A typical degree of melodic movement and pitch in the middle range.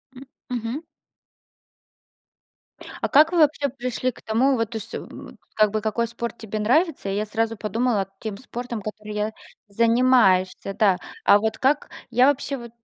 No: average, 3.1 semitones; high, 230 Hz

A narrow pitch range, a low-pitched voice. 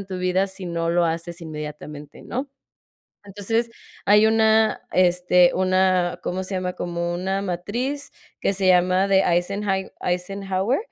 No: narrow, 2.1 semitones; medium, 185 Hz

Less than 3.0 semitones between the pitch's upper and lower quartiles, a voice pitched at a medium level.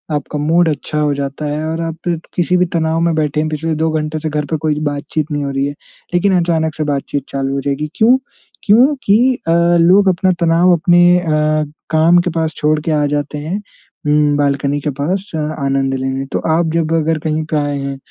Yes: narrow, 2.5 semitones; medium, 155 Hz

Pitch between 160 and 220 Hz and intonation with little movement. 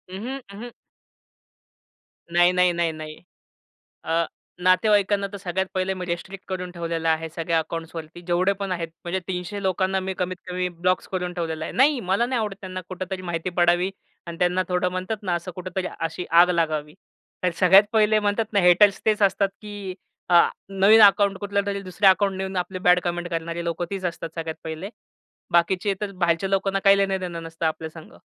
Yes: medium, 185 Hz; narrow, 2.3 semitones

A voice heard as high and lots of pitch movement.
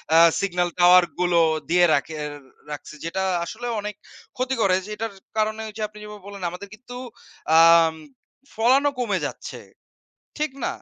No: high, 200 Hz; average, 4.1 semitones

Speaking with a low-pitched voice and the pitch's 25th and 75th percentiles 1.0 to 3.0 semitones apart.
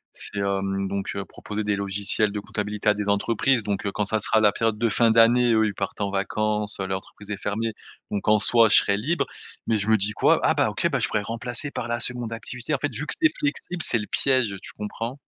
Yes: low, 105 Hz; narrow, 2.4 semitones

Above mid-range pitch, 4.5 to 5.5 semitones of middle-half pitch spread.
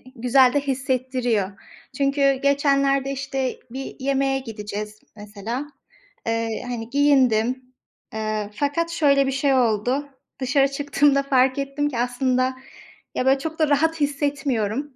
No: very high, 270 Hz; narrow, 2.5 semitones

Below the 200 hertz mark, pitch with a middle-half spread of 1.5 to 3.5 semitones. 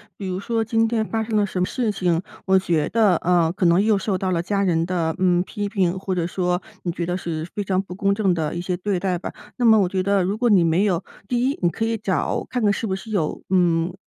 Yes: high, 190 Hz; average, 2.8 semitones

